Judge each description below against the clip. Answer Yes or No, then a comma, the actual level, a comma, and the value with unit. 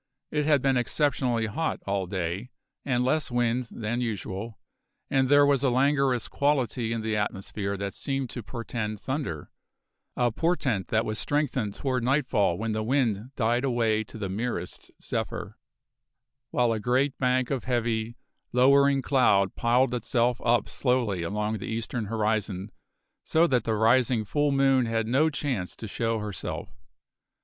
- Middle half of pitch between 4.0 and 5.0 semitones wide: No, average, 3.5 semitones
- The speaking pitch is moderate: No, low, 120 Hz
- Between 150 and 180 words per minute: Yes, average, 155 wpm